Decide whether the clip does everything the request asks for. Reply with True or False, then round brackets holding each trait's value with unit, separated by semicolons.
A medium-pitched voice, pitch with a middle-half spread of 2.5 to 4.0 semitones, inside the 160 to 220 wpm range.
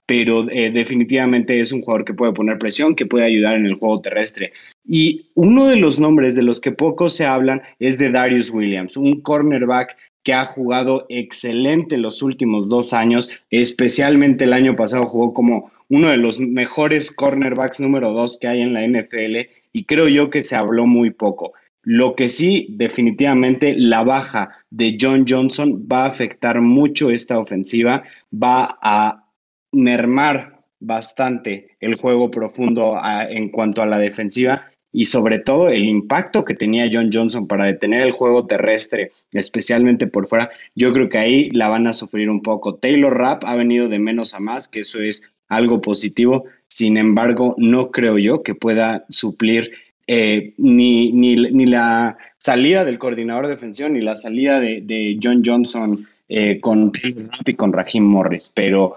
False (120 Hz; 2.8 semitones; 175 wpm)